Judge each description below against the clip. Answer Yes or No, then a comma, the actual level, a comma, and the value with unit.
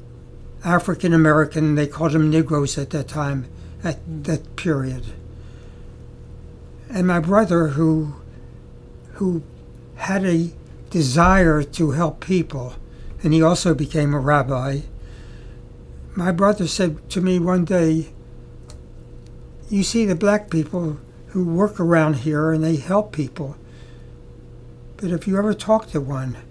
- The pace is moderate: No, slow, 125 wpm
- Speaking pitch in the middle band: Yes, medium, 155 Hz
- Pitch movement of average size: Yes, average, 4.7 semitones